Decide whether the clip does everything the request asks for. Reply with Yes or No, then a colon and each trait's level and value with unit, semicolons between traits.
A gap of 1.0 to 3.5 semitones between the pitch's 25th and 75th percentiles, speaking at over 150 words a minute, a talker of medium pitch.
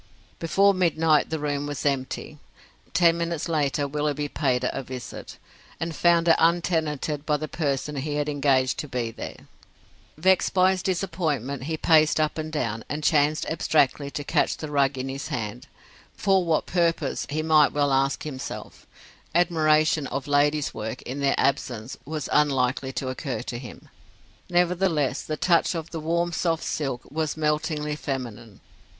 Yes: average, 3.0 semitones; average, 160 wpm; medium, 150 Hz